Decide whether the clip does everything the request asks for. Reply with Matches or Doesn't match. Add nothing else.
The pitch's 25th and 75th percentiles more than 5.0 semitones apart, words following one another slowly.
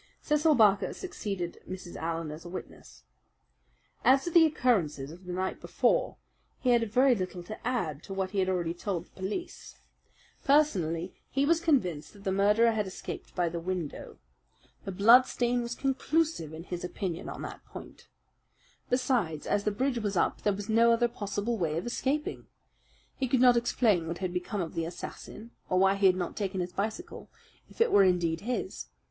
Doesn't match